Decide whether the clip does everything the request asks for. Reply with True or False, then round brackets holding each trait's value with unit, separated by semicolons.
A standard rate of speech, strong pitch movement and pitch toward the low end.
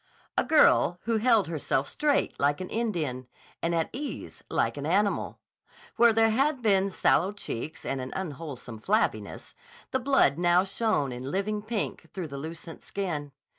False (160 wpm; 7.1 semitones; 185 Hz)